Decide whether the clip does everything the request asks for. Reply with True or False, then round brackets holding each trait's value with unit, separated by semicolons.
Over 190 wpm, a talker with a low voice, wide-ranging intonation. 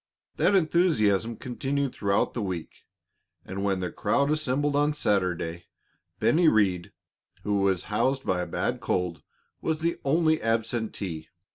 False (135 wpm; 110 Hz; 7.4 semitones)